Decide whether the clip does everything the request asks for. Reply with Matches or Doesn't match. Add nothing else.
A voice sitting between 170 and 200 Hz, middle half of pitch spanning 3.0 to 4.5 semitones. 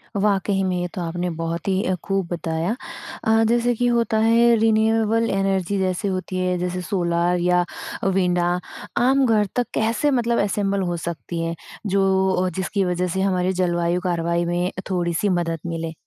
Matches